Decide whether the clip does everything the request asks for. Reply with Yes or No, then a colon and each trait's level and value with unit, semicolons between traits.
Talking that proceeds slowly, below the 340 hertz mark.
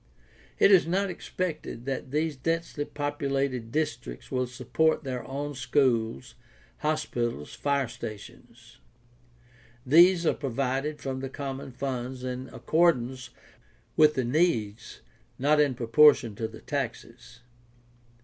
Yes: slow, 120 wpm; low, 135 Hz